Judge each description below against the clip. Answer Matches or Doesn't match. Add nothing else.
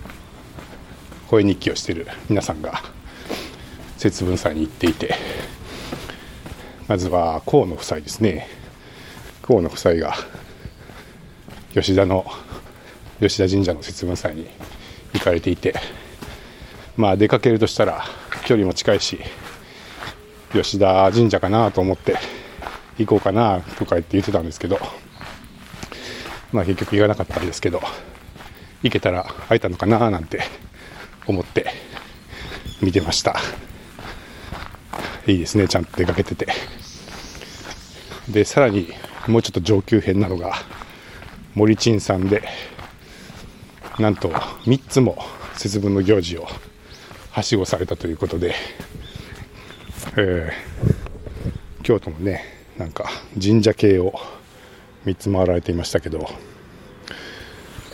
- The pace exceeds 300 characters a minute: Doesn't match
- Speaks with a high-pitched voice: Doesn't match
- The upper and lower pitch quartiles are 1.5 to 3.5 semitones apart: Matches